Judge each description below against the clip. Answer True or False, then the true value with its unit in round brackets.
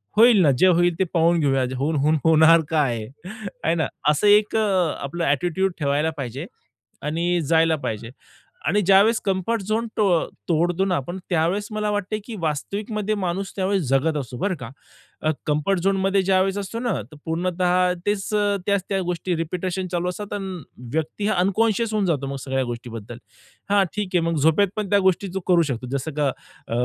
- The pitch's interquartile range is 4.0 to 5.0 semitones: True (4.7 semitones)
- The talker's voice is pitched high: False (175 Hz)